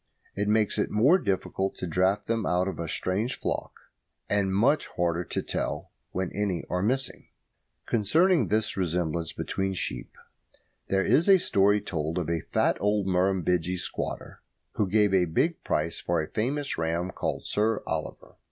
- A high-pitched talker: No, very low, 95 Hz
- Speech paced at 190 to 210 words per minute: No, average, 160 wpm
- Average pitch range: Yes, average, 3.4 semitones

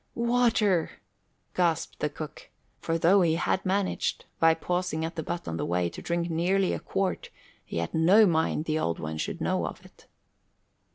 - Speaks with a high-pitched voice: No, medium, 170 Hz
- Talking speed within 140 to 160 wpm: No, average, 180 wpm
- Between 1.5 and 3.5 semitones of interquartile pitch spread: Yes, average, 3.0 semitones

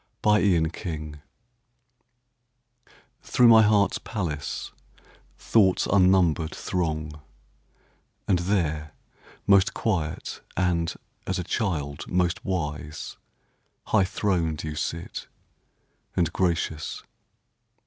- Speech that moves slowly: Yes, slow, 85 wpm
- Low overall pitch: Yes, very low, 85 Hz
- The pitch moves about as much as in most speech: Yes, average, 3.7 semitones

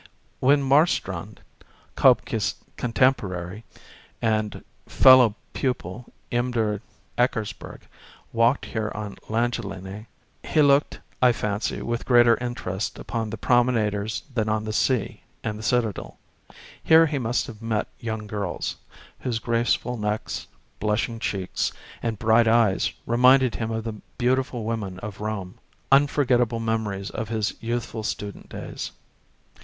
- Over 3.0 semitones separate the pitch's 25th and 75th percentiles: No, narrow, 2.5 semitones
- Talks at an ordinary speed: No, slow, 125 wpm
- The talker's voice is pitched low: Yes, low, 115 Hz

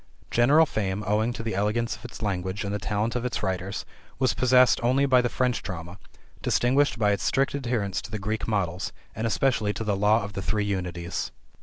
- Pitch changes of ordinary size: Yes, average, 3.7 semitones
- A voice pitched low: Yes, low, 105 Hz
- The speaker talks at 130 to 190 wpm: No, fast, 205 wpm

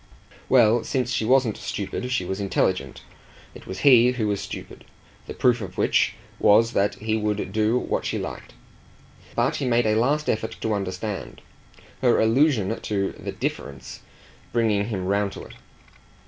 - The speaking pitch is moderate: No, low, 110 Hz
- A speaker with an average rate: Yes, average, 160 wpm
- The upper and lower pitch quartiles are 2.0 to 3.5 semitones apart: Yes, average, 3.2 semitones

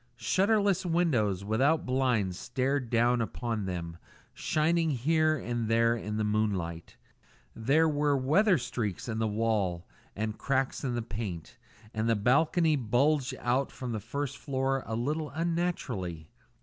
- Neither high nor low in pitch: No, low, 125 Hz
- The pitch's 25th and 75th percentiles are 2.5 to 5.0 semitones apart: No, wide, 5.4 semitones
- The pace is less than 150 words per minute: Yes, average, 140 wpm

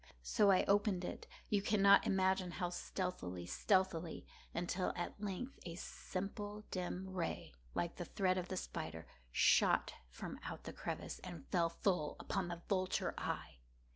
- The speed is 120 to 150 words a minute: Yes, average, 140 wpm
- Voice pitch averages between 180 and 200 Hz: Yes, medium, 185 Hz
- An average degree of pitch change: No, narrow, 2.2 semitones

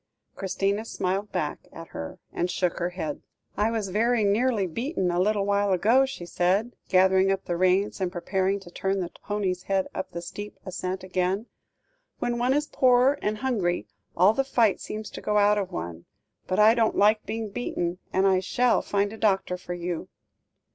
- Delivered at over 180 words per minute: Yes, average, 190 wpm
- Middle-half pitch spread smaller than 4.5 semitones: Yes, average, 3.0 semitones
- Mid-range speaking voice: No, high, 195 Hz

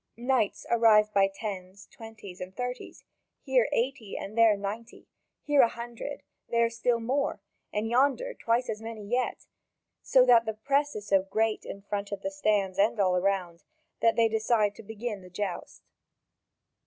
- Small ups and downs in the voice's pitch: No, average, 3.2 semitones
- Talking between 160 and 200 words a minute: Yes, average, 165 wpm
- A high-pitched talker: Yes, high, 225 Hz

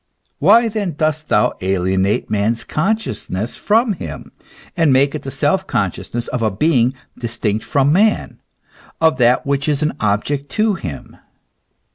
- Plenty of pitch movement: Yes, wide, 6.8 semitones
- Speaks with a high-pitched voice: No, medium, 140 Hz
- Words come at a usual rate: Yes, average, 150 wpm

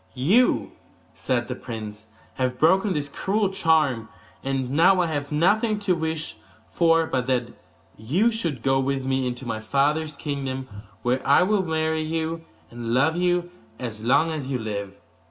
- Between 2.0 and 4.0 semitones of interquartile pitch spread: No, average, 4.7 semitones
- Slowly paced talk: No, average, 160 wpm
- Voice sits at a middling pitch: Yes, medium, 145 Hz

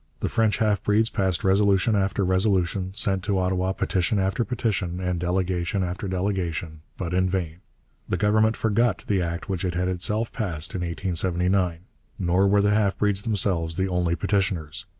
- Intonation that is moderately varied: No, narrow, 2.3 semitones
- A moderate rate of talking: Yes, average, 170 wpm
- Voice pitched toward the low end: Yes, very low, 95 Hz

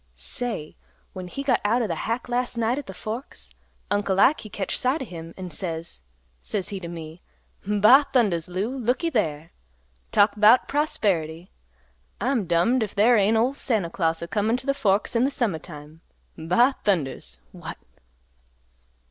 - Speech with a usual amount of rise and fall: No, wide, 6.3 semitones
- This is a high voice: Yes, high, 205 Hz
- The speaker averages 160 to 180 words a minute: Yes, average, 170 wpm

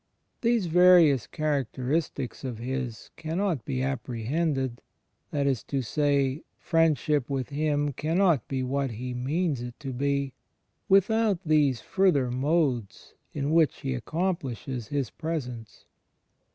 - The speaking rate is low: Yes, slow, 125 wpm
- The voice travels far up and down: No, average, 4.1 semitones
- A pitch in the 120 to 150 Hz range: Yes, medium, 140 Hz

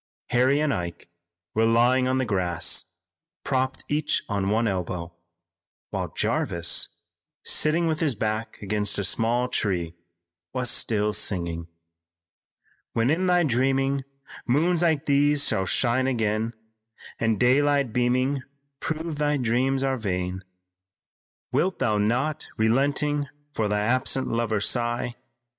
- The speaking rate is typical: No, slow, 125 wpm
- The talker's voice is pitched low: Yes, low, 120 Hz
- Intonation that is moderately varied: Yes, average, 4.8 semitones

